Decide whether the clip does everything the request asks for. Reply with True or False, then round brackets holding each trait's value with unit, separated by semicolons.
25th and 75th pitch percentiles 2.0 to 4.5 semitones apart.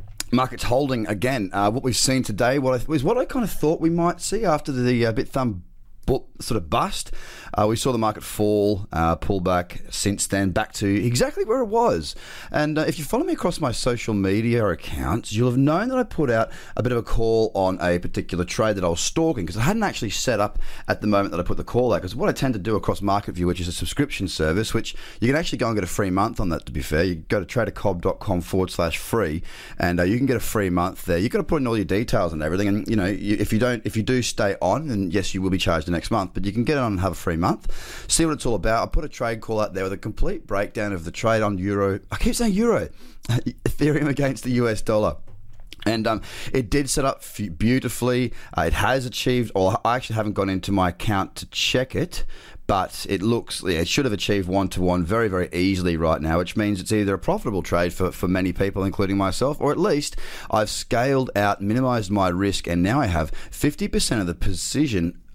False (4.9 semitones)